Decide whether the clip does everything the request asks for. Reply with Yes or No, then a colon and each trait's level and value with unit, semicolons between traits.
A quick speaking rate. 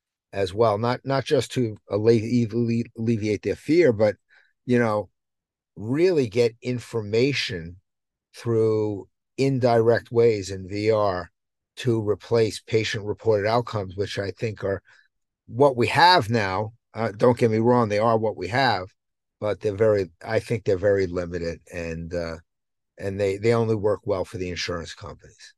No: average, 150 wpm